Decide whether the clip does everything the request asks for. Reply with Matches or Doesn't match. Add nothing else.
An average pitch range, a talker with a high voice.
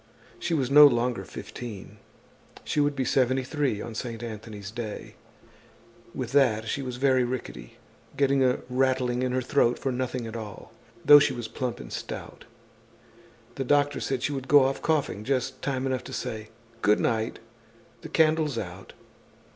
Doesn't match